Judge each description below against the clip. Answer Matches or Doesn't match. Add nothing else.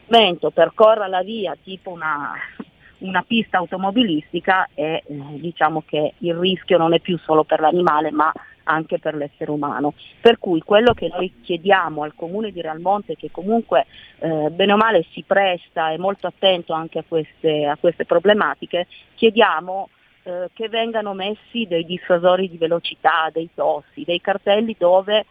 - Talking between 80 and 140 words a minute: Doesn't match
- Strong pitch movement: Doesn't match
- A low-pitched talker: Doesn't match